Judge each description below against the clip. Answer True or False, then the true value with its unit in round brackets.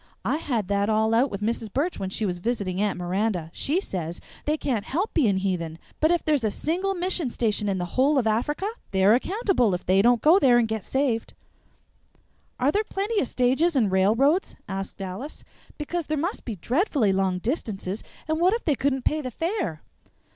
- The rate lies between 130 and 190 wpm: False (200 wpm)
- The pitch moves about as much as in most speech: False (7.7 semitones)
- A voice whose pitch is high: True (240 Hz)